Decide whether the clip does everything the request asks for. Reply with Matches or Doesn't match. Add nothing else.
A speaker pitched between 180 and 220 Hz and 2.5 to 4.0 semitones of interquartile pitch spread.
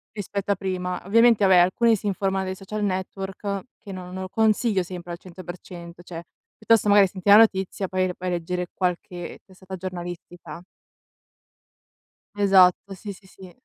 Doesn't match